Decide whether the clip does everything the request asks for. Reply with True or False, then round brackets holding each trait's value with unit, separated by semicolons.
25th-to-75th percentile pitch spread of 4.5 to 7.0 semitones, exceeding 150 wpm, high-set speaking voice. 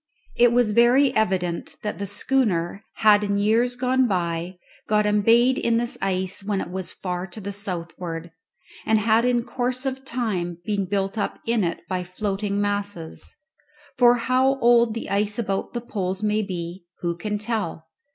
False (4.1 semitones; 170 wpm; 210 Hz)